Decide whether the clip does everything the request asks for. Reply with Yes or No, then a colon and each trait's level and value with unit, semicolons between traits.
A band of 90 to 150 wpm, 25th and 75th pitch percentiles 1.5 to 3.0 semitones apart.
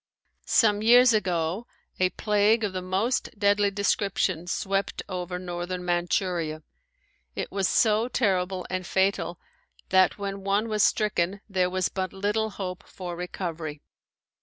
Yes: slow, 135 wpm; narrow, 2.4 semitones